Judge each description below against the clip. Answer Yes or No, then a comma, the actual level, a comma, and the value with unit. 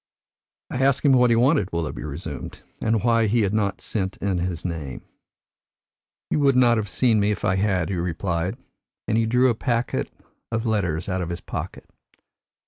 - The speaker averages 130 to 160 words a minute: No, average, 185 wpm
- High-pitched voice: No, low, 105 Hz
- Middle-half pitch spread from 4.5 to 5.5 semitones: Yes, average, 4.8 semitones